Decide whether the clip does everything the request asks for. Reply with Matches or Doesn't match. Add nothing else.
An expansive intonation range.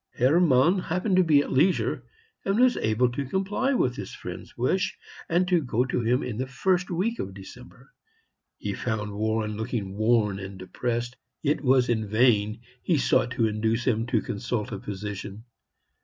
Matches